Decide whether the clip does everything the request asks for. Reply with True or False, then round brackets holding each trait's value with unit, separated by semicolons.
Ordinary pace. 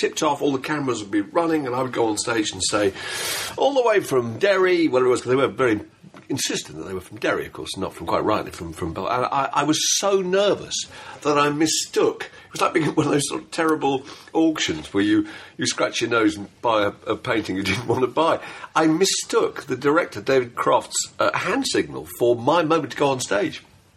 False (240 wpm)